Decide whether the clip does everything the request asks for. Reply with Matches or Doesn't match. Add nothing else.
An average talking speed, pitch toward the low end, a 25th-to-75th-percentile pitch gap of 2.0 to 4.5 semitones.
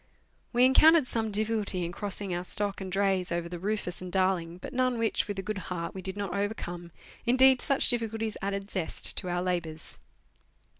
Doesn't match